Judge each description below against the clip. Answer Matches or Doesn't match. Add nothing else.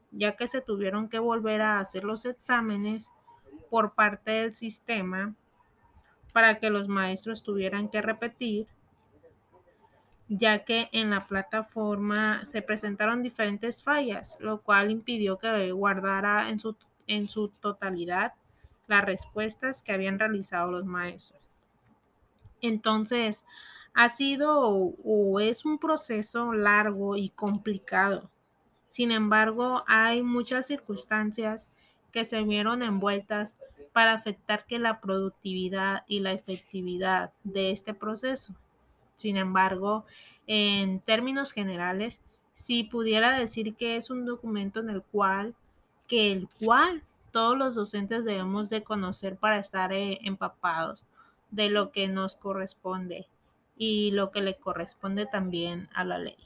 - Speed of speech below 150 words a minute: Matches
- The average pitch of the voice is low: Doesn't match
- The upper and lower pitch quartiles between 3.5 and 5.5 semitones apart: Doesn't match